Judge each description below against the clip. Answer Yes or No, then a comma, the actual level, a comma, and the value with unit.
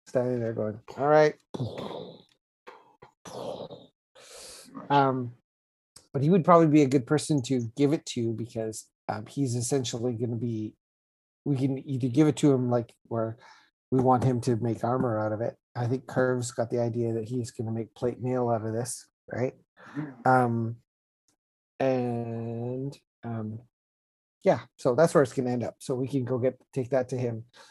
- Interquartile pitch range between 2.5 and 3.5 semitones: Yes, average, 2.9 semitones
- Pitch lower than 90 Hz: No, low, 125 Hz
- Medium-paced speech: Yes, average, 175 wpm